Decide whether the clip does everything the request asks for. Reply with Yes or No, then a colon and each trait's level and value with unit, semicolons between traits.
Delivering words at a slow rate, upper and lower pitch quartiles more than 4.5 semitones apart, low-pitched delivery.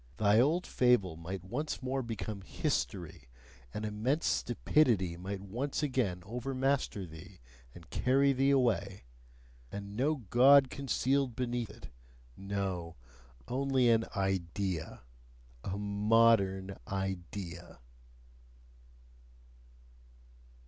Yes: slow, 95 wpm; average, 5.2 semitones; low, 105 Hz